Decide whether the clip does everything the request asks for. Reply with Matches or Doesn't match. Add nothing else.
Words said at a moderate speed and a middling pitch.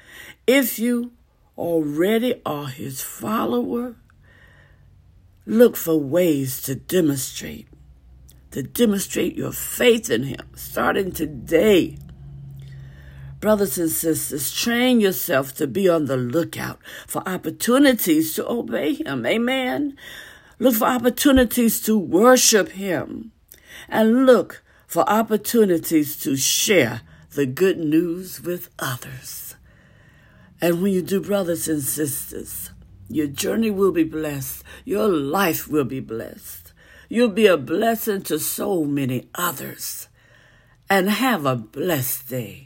Doesn't match